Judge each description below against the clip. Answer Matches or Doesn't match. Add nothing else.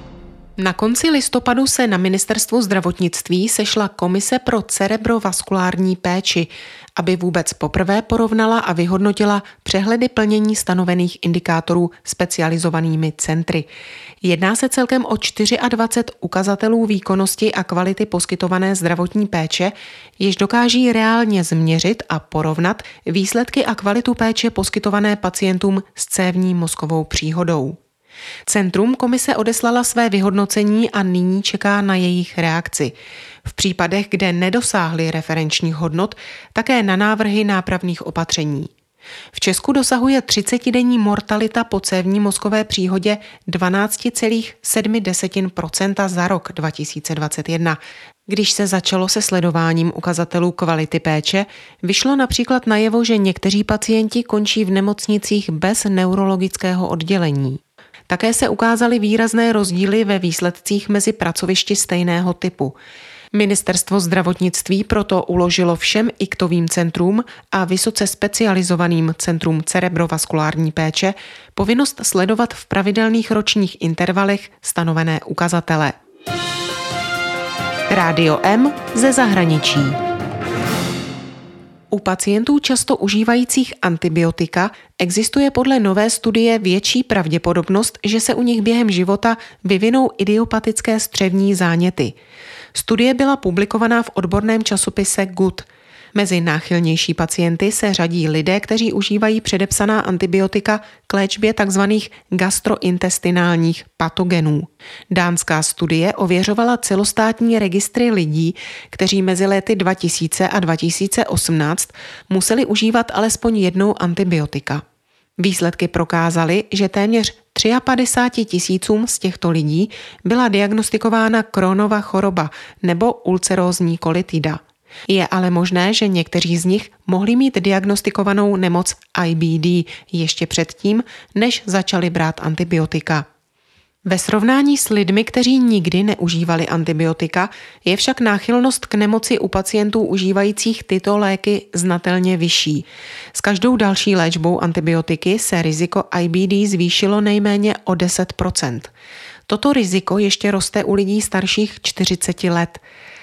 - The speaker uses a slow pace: Matches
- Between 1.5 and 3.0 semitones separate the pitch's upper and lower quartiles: Doesn't match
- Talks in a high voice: Matches